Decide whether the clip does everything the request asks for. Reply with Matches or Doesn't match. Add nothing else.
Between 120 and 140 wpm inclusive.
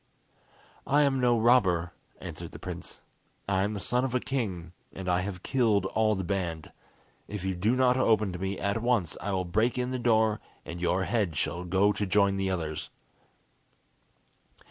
Doesn't match